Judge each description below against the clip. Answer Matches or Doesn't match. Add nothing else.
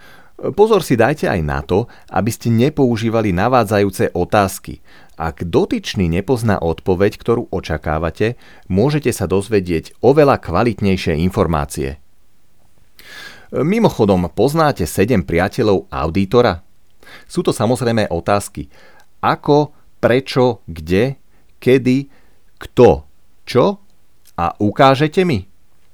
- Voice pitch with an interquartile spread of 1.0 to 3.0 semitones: Doesn't match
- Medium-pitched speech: Doesn't match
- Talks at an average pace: Doesn't match